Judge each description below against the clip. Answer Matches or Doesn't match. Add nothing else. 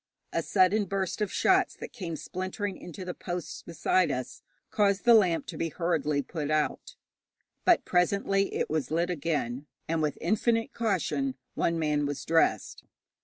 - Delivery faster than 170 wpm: Doesn't match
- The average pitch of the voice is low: Doesn't match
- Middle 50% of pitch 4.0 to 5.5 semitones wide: Matches